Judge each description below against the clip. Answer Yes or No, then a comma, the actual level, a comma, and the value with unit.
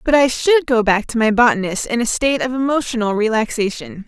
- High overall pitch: Yes, high, 240 Hz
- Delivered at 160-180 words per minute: No, fast, 205 wpm